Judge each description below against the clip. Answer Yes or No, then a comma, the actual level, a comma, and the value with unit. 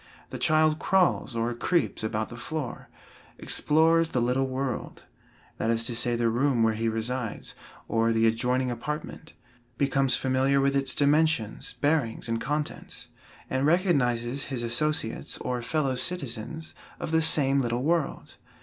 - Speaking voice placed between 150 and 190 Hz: No, low, 130 Hz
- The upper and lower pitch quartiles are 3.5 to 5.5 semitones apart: Yes, average, 4.4 semitones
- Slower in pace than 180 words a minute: Yes, average, 145 wpm